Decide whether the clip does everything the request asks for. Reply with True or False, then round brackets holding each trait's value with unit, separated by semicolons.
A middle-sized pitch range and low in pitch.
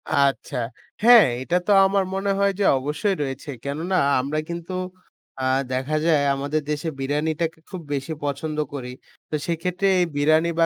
False (3.9 semitones; 155 Hz)